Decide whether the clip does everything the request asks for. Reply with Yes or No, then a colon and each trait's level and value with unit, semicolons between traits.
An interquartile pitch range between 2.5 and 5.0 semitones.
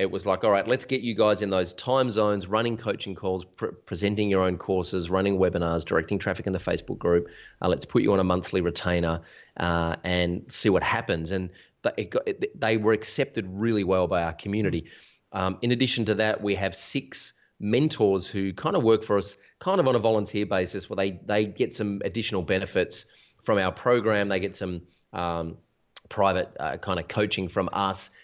Yes: average, 3.0 semitones